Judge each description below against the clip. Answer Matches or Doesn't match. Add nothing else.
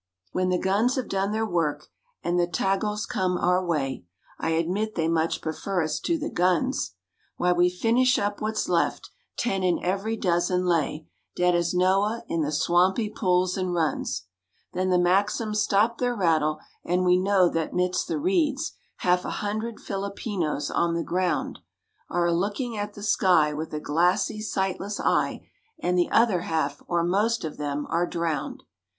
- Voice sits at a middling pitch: Matches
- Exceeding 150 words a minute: Matches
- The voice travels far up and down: Doesn't match